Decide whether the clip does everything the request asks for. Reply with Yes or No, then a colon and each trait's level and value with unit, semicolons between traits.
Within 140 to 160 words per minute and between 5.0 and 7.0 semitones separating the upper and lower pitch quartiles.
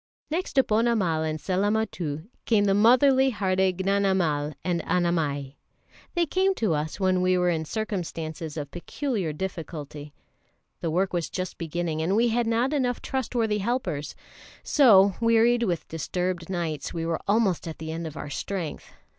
Yes: average, 155 wpm; wide, 5.6 semitones